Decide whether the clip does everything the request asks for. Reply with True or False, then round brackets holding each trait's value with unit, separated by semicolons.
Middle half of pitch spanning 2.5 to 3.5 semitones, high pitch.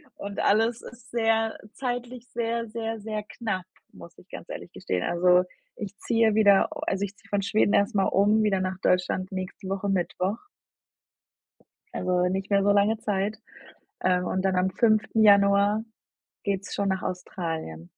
True (2.8 semitones; 200 Hz)